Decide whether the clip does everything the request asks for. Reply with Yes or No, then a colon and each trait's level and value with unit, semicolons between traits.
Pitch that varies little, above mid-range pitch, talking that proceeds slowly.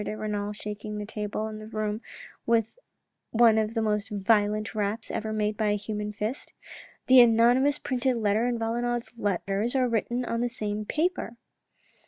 No: narrow, 2.1 semitones; high, 220 Hz; average, 170 wpm